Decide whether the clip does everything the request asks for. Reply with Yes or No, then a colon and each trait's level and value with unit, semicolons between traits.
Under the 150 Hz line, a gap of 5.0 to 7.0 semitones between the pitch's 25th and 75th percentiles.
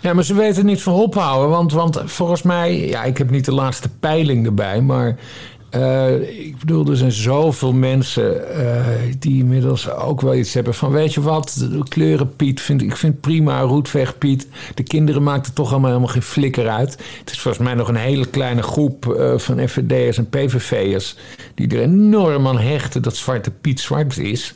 No: low, 135 Hz; average, 3.4 semitones